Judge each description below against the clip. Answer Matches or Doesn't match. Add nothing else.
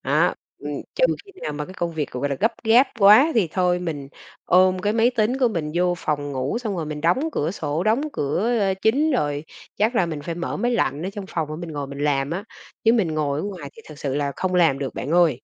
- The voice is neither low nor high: Matches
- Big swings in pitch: Matches